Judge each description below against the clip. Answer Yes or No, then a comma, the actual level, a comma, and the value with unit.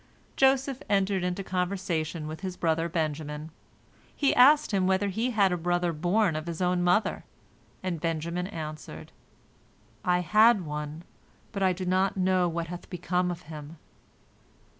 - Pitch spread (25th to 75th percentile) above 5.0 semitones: No, average, 2.8 semitones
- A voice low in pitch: No, medium, 180 Hz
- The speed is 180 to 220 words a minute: No, average, 150 wpm